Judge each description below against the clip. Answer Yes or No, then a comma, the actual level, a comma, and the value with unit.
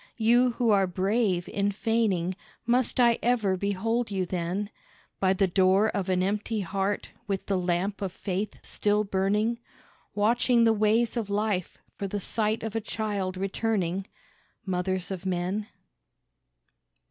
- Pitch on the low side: No, high, 200 Hz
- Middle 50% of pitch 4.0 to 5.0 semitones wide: No, average, 2.9 semitones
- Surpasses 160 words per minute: No, average, 145 wpm